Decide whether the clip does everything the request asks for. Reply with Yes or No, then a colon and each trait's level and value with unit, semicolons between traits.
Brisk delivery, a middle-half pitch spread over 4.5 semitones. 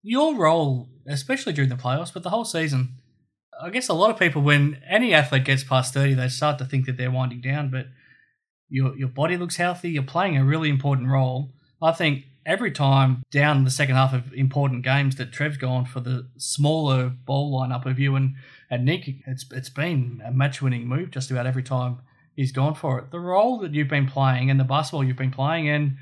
No: fast, 215 wpm; average, 2.8 semitones